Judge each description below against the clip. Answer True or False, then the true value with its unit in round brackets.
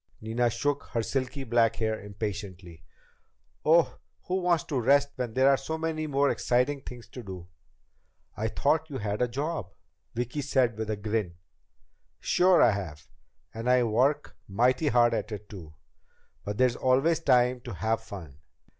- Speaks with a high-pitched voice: False (120 Hz)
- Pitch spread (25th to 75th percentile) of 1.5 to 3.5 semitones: False (4.6 semitones)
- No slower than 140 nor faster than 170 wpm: True (165 wpm)